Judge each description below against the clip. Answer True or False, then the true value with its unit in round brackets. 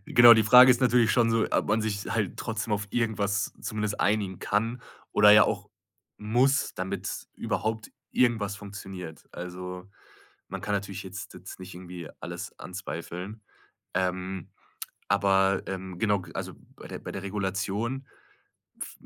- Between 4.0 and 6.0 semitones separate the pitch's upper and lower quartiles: False (2.8 semitones)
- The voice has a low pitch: True (100 Hz)